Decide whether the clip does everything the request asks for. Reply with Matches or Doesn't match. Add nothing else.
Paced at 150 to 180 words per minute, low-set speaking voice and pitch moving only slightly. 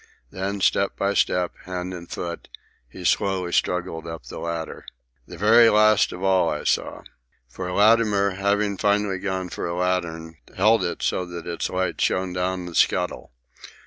Matches